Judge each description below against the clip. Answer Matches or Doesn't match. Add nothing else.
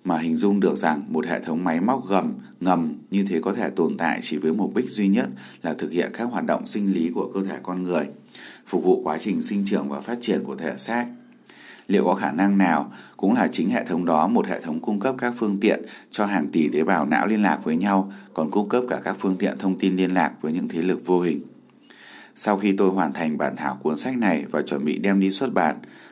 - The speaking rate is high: Matches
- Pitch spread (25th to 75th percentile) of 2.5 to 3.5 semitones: Matches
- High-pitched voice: Doesn't match